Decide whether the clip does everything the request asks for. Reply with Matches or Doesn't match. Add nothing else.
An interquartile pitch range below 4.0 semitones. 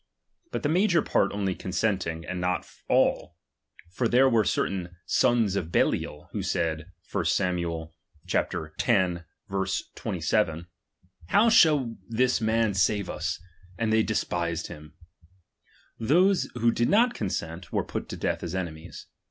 Doesn't match